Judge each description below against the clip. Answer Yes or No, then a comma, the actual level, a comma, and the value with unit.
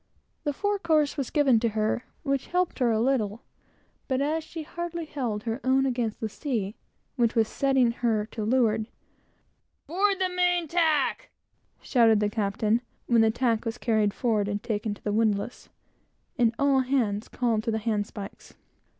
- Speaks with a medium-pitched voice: No, high, 240 Hz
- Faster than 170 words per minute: No, average, 165 wpm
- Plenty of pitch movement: No, average, 4.6 semitones